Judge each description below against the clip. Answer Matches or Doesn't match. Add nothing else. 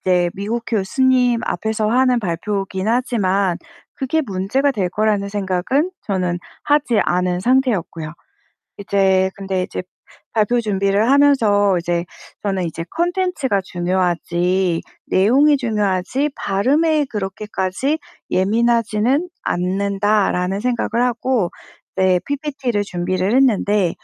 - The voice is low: Doesn't match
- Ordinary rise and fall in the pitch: Matches